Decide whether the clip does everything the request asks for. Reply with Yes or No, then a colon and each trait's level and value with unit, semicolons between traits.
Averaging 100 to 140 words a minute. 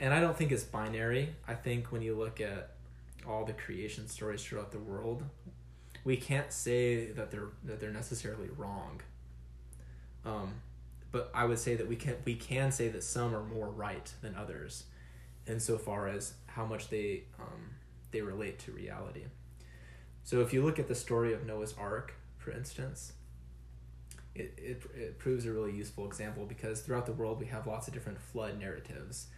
No: average, 180 wpm